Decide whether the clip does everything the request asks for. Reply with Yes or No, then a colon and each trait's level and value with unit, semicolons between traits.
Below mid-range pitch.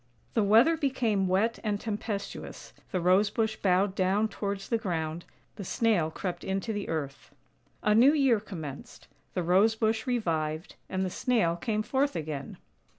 No: high, 200 Hz